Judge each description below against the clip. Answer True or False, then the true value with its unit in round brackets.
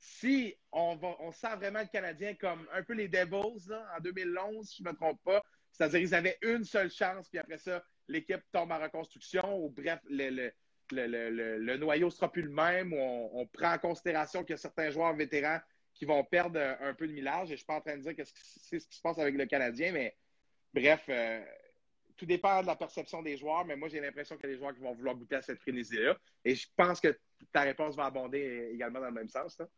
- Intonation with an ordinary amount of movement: True (4.6 semitones)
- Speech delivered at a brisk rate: True (250 wpm)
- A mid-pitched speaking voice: True (160 Hz)